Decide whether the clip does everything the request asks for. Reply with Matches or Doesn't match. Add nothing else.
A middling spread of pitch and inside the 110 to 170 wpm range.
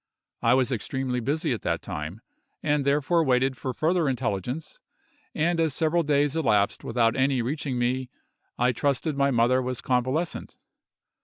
Matches